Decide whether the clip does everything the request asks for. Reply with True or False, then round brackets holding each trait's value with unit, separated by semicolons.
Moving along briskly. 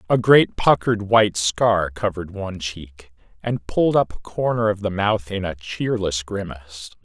False (170 wpm)